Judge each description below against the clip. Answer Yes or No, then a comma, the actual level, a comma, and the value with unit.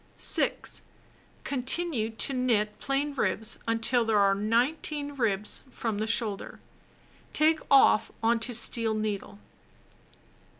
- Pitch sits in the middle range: No, high, 230 Hz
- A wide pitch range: No, average, 4.1 semitones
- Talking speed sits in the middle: No, slow, 115 wpm